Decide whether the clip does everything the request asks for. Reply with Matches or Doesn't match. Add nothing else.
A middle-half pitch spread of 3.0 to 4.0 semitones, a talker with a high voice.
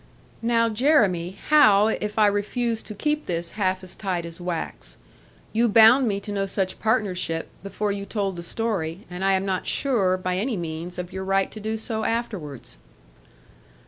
Matches